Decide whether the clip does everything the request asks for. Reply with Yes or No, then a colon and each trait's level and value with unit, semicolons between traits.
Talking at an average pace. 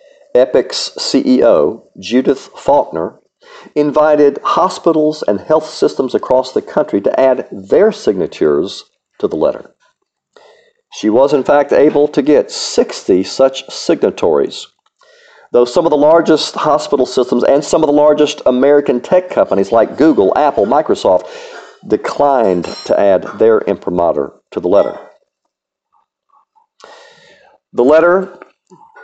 No: slow, 120 wpm